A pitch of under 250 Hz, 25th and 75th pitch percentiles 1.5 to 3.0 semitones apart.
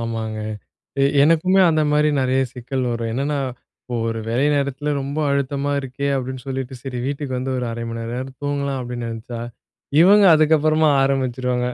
Yes: low, 135 Hz; narrow, 2.6 semitones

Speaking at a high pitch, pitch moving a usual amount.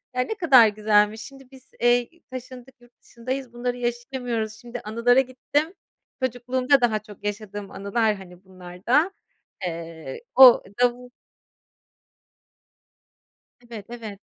Yes: high, 240 Hz; average, 3.3 semitones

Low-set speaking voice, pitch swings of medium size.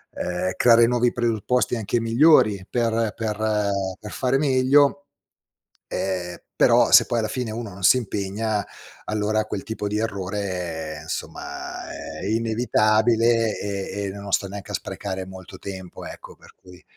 Yes: low, 105 Hz; average, 3.1 semitones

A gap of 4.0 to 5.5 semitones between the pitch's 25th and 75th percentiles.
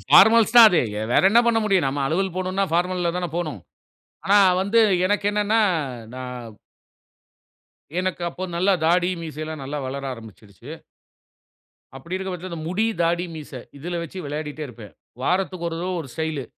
Yes: average, 4.3 semitones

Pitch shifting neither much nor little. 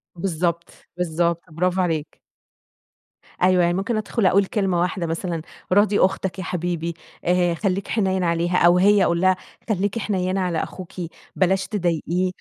No: narrow, 2.0 semitones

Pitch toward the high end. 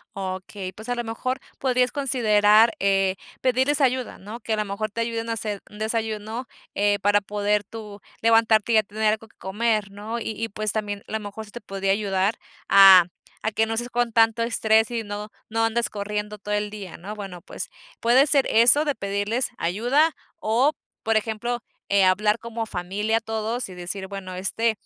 Yes: high, 215 Hz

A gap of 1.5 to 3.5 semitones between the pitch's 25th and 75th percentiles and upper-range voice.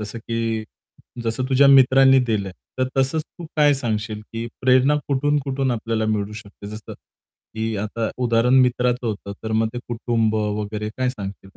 No: average, 3.2 semitones; low, 115 Hz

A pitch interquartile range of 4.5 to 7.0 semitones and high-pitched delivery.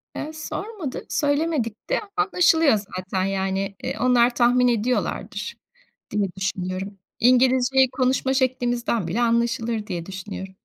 Yes: average, 5.0 semitones; high, 240 Hz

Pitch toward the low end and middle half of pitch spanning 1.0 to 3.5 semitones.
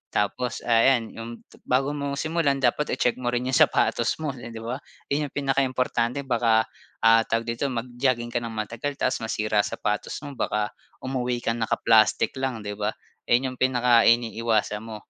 Yes: low, 120 Hz; narrow, 2.6 semitones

